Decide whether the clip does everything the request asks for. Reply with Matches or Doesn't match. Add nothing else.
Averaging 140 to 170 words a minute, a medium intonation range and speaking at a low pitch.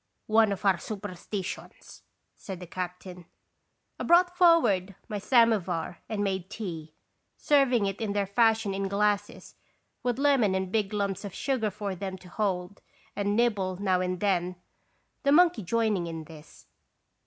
Doesn't match